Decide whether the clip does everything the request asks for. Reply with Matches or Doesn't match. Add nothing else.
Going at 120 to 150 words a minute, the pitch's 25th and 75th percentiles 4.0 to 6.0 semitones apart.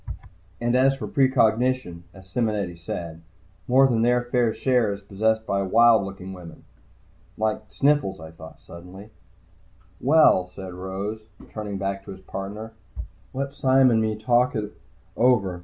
Matches